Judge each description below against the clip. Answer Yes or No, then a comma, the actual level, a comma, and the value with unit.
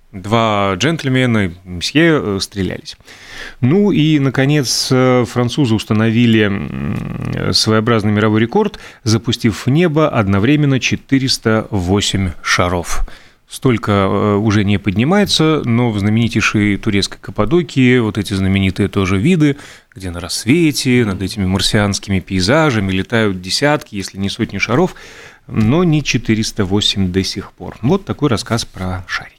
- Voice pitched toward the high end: No, low, 110 Hz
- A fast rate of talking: No, average, 115 wpm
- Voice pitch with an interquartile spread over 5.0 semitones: No, average, 4.7 semitones